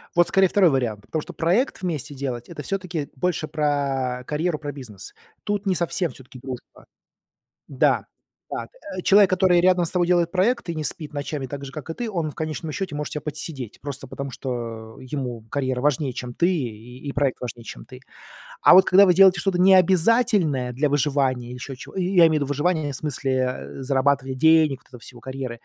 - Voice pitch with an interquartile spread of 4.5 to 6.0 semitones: Yes, average, 5.2 semitones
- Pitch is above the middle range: No, medium, 145 Hz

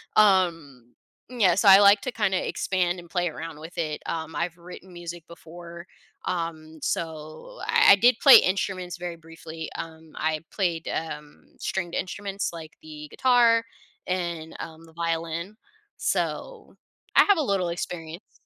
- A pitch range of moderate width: Yes, average, 3.0 semitones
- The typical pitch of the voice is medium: Yes, medium, 170 Hz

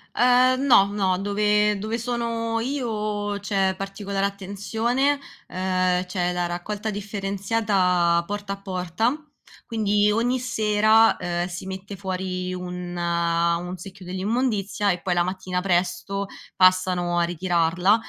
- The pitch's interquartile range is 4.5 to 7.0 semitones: No, average, 2.8 semitones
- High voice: Yes, high, 195 Hz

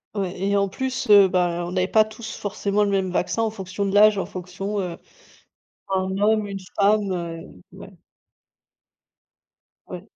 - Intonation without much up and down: Yes, narrow, 2.1 semitones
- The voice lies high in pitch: Yes, high, 195 Hz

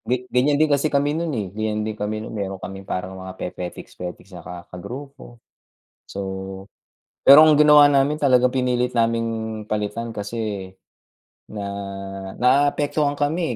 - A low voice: Yes, low, 115 Hz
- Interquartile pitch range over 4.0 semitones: Yes, wide, 5.5 semitones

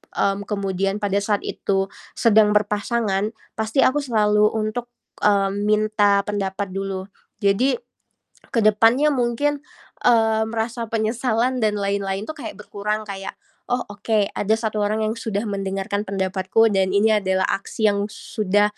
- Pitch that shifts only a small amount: Yes, narrow, 2.0 semitones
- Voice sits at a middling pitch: No, high, 210 Hz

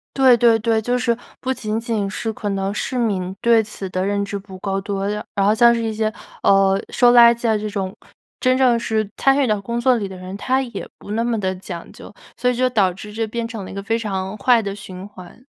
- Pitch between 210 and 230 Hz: Yes, high, 215 Hz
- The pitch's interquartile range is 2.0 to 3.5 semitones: Yes, average, 3.2 semitones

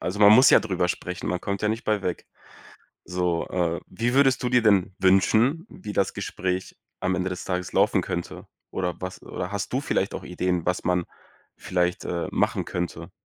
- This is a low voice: Yes, very low, 95 Hz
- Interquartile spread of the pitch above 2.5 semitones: Yes, average, 2.9 semitones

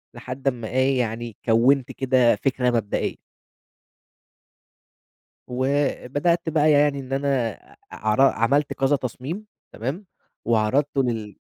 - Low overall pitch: Yes, low, 130 Hz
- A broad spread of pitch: No, average, 3.2 semitones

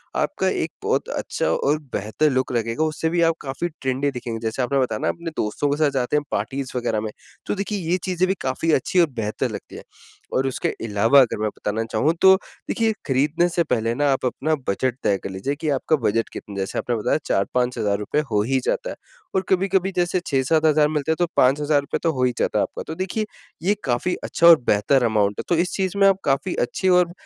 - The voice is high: No, medium, 140 Hz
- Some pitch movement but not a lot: No, wide, 5.9 semitones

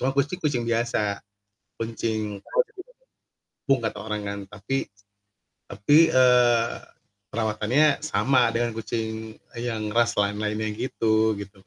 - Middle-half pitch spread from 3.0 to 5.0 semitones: No, narrow, 2.6 semitones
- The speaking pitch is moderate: No, low, 115 Hz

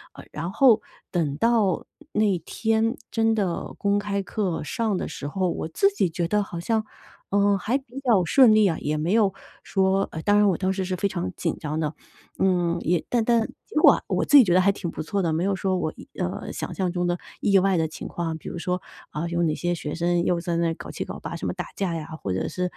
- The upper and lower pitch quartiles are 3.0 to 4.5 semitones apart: Yes, average, 3.5 semitones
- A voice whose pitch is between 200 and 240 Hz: No, medium, 185 Hz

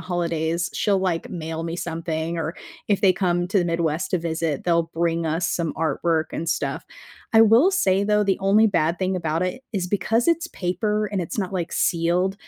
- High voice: No, medium, 175 Hz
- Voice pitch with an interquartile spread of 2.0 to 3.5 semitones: Yes, average, 2.9 semitones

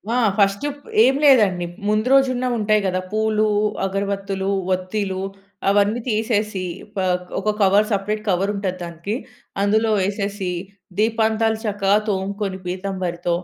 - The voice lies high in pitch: Yes, high, 200 Hz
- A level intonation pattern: Yes, narrow, 2.2 semitones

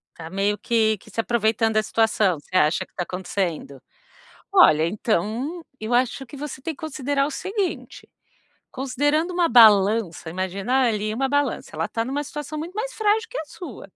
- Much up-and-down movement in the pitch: Yes, wide, 6.4 semitones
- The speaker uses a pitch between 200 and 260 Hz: Yes, high, 235 Hz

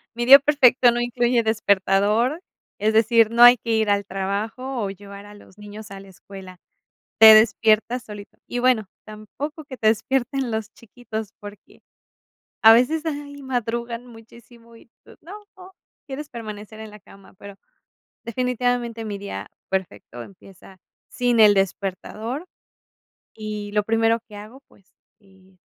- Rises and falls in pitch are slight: No, average, 3.1 semitones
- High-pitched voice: Yes, high, 220 Hz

